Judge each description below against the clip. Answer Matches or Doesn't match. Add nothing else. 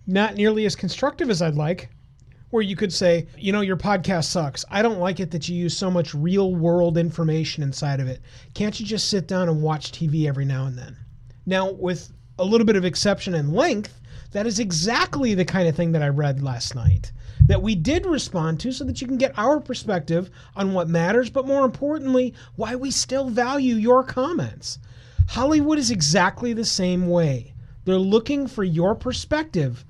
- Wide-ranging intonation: Matches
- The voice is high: Doesn't match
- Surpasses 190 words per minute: Matches